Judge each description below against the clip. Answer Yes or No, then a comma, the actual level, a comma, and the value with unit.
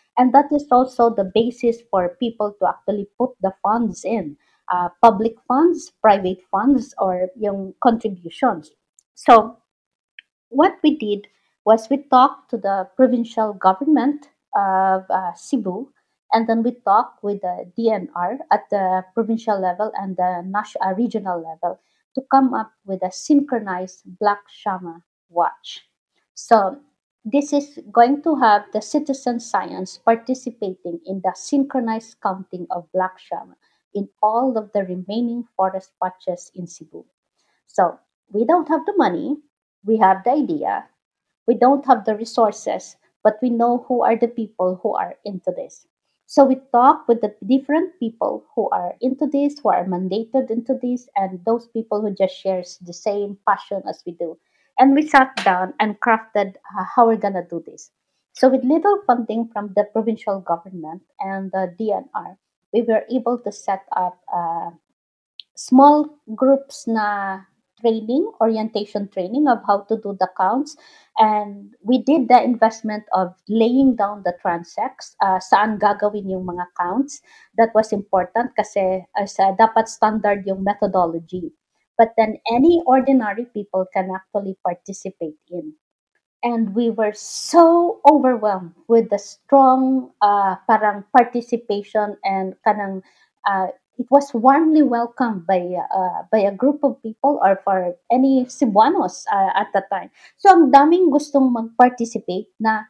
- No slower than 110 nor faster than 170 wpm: Yes, average, 150 wpm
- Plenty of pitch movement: No, average, 4.8 semitones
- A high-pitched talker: Yes, high, 220 Hz